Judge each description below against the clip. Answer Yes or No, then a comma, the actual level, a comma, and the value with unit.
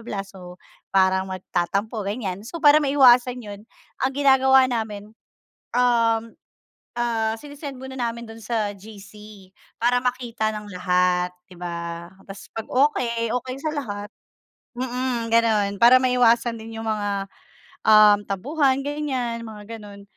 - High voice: Yes, high, 230 Hz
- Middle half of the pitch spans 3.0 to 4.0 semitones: Yes, average, 3.7 semitones